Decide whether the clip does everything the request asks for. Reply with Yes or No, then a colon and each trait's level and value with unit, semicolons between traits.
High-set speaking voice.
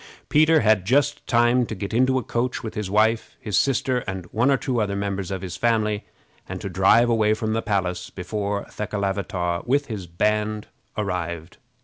No: low, 105 Hz